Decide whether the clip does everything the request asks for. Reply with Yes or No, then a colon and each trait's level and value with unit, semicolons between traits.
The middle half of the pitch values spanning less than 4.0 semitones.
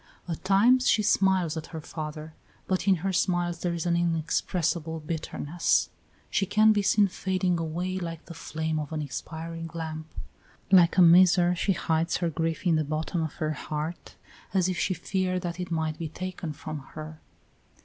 Yes: narrow, 2.6 semitones